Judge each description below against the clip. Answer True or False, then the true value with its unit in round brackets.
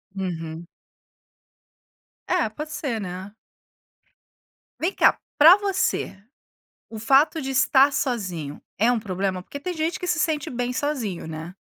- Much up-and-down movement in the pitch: True (8.5 semitones)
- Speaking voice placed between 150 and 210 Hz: False (245 Hz)